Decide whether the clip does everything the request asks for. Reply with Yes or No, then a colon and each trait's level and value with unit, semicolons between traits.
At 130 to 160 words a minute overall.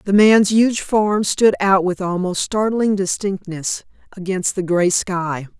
Yes: average, 150 wpm